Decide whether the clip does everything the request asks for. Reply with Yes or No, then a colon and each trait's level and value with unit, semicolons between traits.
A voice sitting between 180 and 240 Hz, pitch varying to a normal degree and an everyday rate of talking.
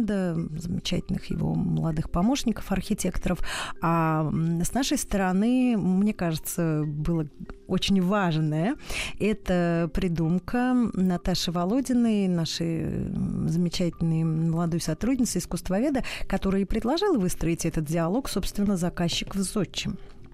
No: medium, 185 Hz; average, 3.5 semitones; slow, 95 wpm